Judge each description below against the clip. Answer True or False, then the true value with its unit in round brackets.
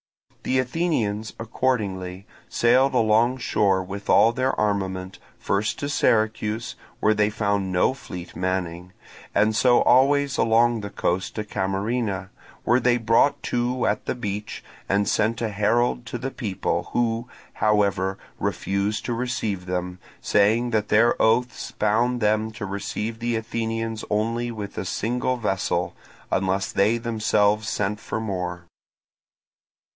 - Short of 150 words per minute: True (135 wpm)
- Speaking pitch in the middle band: False (110 Hz)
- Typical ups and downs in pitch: True (3.1 semitones)